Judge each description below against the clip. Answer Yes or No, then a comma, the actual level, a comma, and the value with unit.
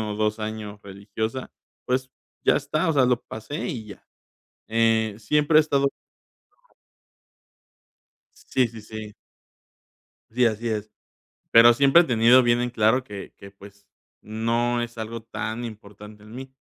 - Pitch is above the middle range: No, low, 115 Hz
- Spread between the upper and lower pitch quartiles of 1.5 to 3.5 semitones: Yes, average, 2.8 semitones